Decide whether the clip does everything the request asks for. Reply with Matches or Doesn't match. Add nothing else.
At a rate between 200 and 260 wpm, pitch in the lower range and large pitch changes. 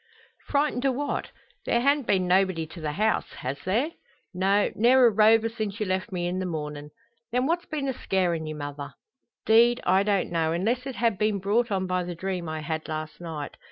Doesn't match